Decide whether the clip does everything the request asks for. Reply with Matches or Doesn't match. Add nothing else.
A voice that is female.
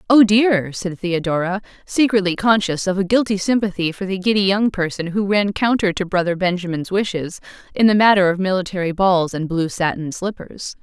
Matches